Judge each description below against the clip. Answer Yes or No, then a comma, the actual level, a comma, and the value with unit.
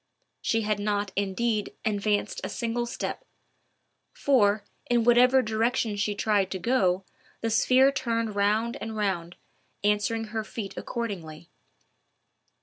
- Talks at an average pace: No, slow, 125 wpm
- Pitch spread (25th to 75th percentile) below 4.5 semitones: Yes, narrow, 2.5 semitones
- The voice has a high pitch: Yes, high, 215 Hz